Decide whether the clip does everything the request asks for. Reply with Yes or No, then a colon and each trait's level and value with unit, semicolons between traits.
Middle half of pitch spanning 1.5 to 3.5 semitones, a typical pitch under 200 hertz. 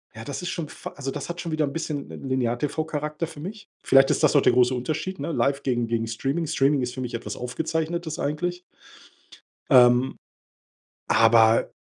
No: average, 4.4 semitones; medium, 140 Hz